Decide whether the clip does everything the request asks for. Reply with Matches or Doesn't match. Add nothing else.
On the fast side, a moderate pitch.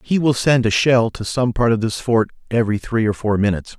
Doesn't match